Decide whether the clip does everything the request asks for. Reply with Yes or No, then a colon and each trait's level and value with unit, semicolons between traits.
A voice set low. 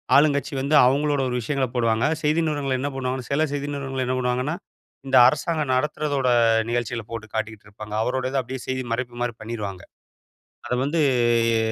Yes: low, 130 Hz